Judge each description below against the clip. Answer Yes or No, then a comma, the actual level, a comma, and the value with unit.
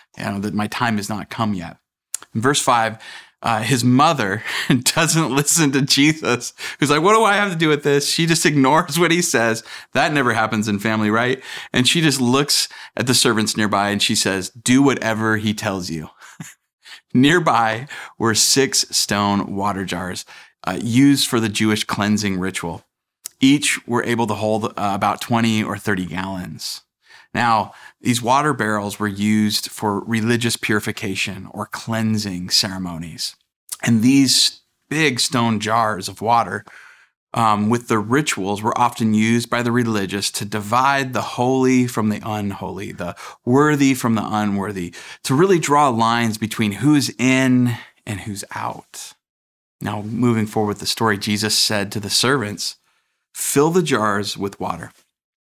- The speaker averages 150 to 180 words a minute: Yes, average, 160 wpm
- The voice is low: Yes, low, 110 Hz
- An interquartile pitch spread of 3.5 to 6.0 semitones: Yes, average, 3.9 semitones